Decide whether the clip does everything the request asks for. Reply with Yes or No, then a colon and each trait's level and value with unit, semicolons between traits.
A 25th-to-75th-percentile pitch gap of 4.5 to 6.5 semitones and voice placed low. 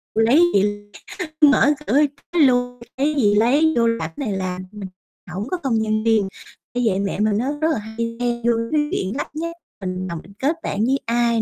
No: average, 4.8 semitones; high, 230 Hz